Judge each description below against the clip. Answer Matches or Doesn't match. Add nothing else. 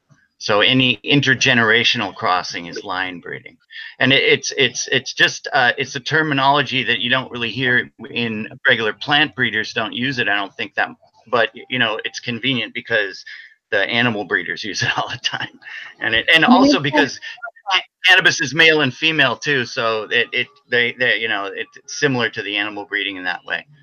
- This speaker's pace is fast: Doesn't match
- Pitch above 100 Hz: Matches